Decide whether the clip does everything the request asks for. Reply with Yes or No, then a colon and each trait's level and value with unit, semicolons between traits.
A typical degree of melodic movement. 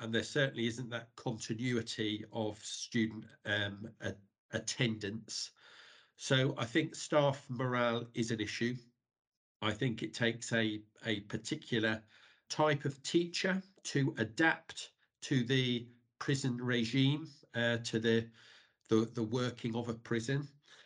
Yes: average, 3.2 semitones